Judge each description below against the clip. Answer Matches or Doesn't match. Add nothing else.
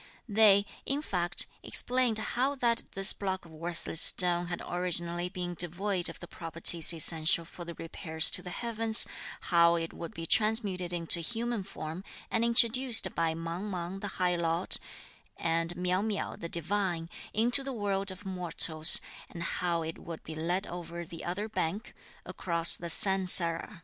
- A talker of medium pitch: Matches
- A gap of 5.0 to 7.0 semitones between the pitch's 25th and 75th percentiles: Doesn't match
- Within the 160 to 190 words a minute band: Matches